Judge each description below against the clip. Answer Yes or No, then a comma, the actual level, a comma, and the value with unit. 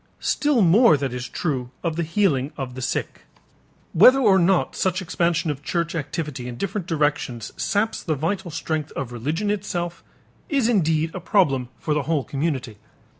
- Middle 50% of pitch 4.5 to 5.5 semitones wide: Yes, average, 5.2 semitones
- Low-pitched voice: No, medium, 165 Hz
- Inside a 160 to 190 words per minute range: Yes, average, 170 wpm